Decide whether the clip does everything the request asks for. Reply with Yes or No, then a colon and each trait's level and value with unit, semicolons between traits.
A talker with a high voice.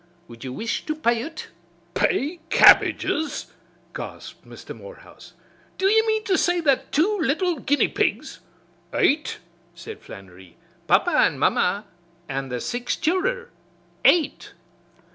Yes: very high, 305 Hz